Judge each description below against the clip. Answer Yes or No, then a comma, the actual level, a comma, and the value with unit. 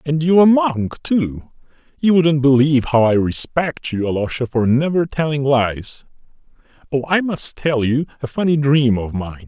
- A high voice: No, medium, 140 Hz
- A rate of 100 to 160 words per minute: No, average, 170 wpm